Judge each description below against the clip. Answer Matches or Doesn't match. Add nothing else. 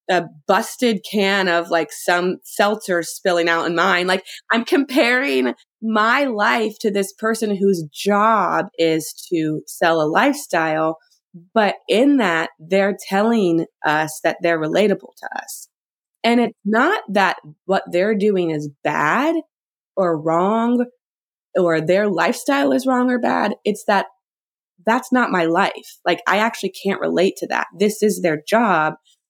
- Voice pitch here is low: Doesn't match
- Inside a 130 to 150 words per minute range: Matches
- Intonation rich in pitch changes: Doesn't match